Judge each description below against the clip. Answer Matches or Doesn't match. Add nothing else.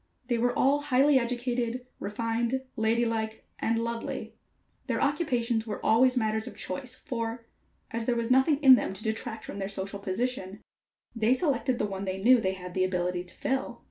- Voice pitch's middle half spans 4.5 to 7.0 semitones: Doesn't match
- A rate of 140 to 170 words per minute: Doesn't match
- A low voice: Doesn't match